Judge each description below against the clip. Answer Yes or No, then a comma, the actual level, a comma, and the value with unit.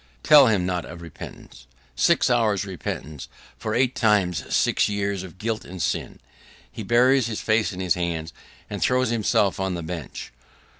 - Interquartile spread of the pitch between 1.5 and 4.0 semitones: No, average, 4.4 semitones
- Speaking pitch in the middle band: No, low, 100 Hz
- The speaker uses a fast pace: No, average, 165 wpm